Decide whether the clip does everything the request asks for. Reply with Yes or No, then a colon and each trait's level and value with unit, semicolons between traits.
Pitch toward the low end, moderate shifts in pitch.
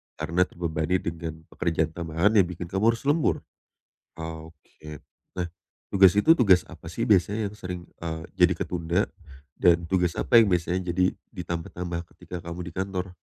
No: very low, 90 Hz; narrow, 2.3 semitones